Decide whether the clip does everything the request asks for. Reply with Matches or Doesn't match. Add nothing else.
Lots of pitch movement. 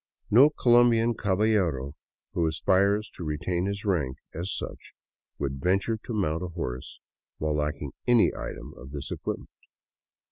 Matches